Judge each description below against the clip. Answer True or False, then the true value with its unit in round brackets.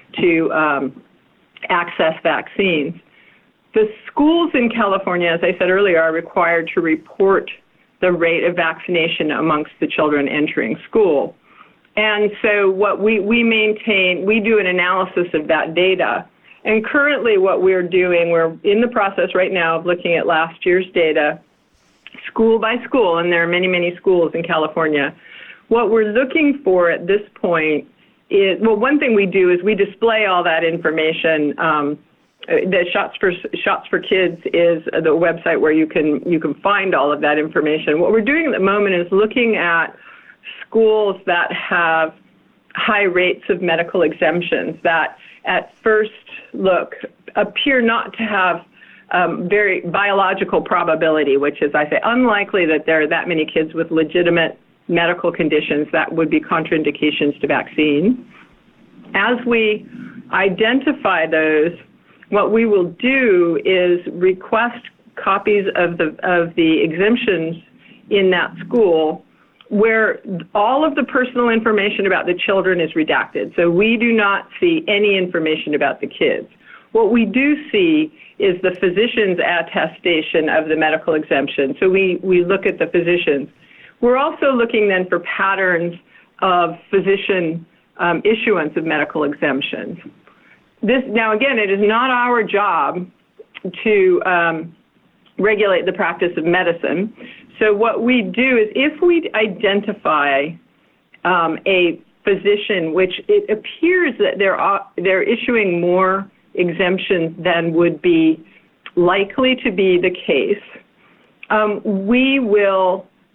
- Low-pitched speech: False (190 Hz)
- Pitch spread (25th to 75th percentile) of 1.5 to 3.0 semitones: False (4.8 semitones)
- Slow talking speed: False (145 wpm)